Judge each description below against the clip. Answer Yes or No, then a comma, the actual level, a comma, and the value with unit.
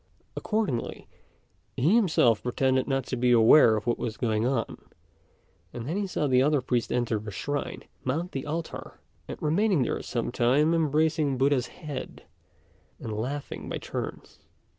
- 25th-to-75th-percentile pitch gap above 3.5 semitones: Yes, average, 4.3 semitones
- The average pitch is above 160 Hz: No, low, 135 Hz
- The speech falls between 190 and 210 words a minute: No, average, 155 wpm